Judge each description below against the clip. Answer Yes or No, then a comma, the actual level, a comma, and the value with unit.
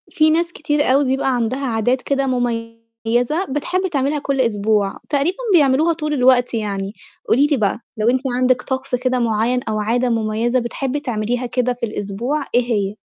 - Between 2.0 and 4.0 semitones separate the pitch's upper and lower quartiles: Yes, average, 3.3 semitones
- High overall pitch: Yes, very high, 250 Hz